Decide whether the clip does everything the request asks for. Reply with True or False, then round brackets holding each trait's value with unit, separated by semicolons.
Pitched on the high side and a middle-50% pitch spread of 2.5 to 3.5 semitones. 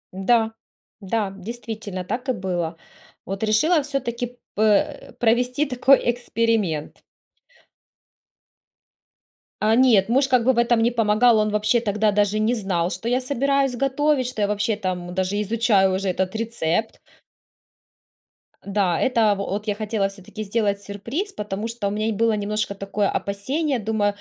True (215 Hz; 3.2 semitones)